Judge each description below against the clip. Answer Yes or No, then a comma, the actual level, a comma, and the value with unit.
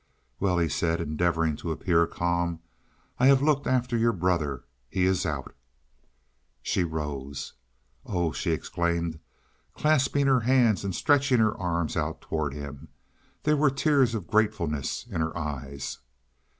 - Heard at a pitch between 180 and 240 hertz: No, very low, 85 Hz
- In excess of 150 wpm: No, average, 140 wpm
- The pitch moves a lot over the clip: Yes, wide, 6.9 semitones